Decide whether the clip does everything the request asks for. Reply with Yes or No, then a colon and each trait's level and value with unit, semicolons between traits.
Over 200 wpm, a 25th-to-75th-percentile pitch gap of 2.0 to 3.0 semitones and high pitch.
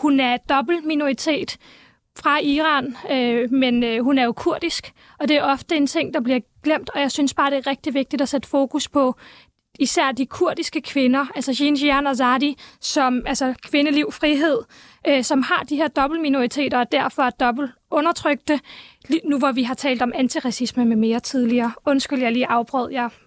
No: average, 190 wpm; average, 2.7 semitones; very high, 275 Hz